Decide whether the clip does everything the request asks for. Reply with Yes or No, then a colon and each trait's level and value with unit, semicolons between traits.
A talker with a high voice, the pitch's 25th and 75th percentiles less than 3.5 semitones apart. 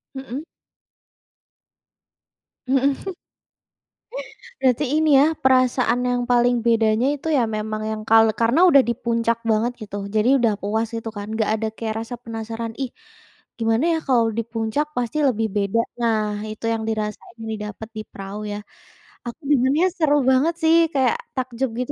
Yes: high, 230 Hz; average, 2.9 semitones